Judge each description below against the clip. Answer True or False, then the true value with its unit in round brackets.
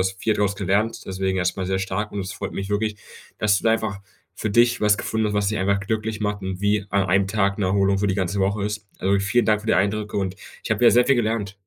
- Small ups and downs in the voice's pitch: True (1.9 semitones)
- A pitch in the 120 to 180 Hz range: False (100 Hz)